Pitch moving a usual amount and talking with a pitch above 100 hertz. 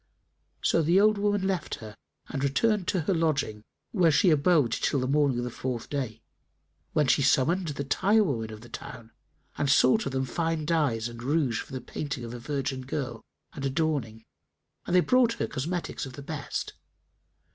Yes: average, 4.8 semitones; medium, 140 Hz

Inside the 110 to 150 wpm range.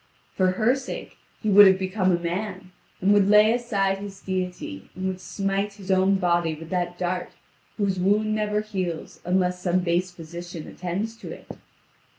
No: average, 170 wpm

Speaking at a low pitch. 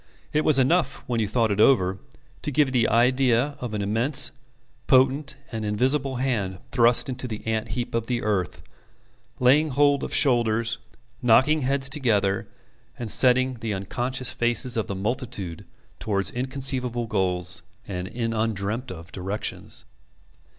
Yes: low, 120 Hz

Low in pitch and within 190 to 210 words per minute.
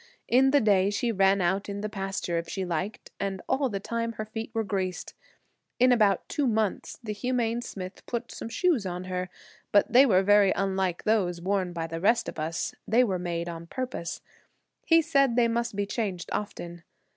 No: high, 200 Hz; average, 195 wpm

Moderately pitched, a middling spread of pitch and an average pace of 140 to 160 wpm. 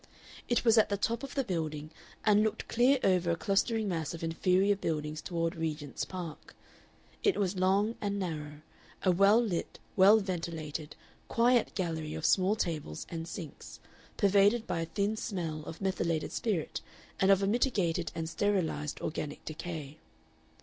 Yes: medium, 180 Hz; average, 4.1 semitones; average, 155 wpm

